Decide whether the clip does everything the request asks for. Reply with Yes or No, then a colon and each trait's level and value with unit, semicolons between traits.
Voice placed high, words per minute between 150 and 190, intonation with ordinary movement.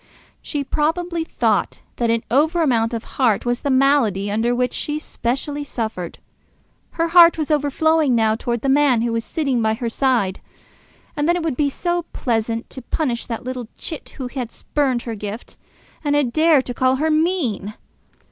Yes: very high, 260 Hz; average, 180 wpm; average, 4.6 semitones